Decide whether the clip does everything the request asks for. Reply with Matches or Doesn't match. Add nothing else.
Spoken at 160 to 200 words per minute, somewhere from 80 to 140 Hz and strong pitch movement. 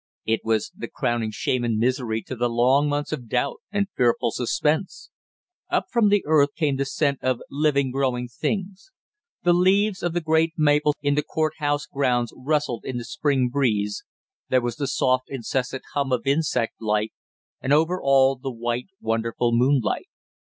Doesn't match